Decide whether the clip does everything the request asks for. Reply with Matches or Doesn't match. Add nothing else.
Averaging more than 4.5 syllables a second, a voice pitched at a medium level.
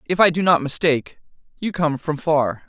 Matches